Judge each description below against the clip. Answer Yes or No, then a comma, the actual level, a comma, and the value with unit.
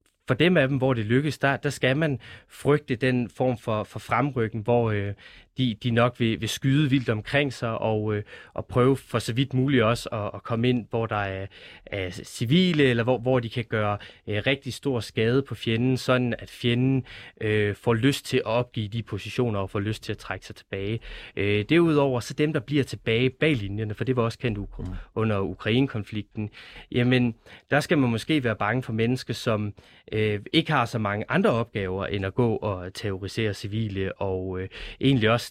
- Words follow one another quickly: No, average, 205 wpm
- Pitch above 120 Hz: No, low, 115 Hz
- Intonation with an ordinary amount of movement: Yes, average, 3.6 semitones